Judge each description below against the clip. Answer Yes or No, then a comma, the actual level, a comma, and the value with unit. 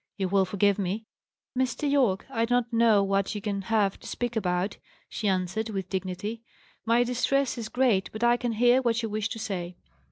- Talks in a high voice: Yes, high, 220 Hz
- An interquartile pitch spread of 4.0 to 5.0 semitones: No, average, 3.5 semitones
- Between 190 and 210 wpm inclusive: Yes, average, 200 wpm